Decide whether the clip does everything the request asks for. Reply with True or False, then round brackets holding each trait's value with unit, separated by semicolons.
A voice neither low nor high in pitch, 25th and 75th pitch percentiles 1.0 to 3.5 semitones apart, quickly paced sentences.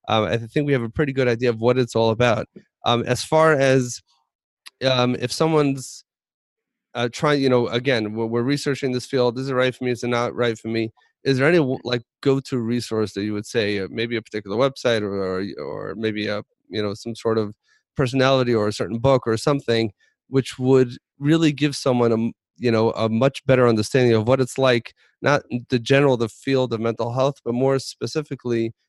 False (125 Hz; 2.8 semitones; 210 wpm)